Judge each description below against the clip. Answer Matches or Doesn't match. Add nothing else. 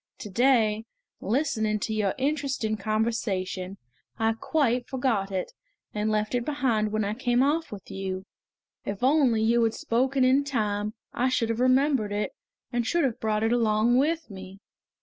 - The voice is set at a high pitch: Matches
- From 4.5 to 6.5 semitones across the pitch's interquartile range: Doesn't match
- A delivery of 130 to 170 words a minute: Matches